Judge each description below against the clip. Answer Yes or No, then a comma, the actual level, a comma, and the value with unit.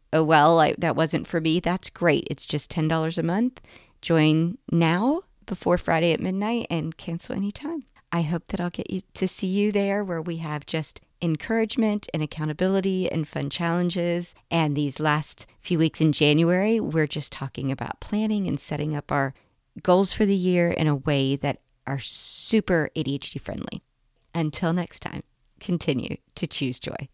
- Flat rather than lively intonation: No, average, 3.8 semitones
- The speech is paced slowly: No, average, 170 wpm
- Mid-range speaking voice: Yes, medium, 165 Hz